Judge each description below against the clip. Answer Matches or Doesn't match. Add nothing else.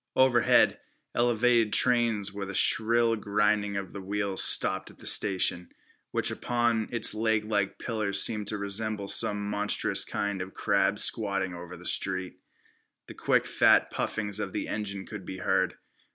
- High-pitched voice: Doesn't match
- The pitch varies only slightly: Matches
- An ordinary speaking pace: Matches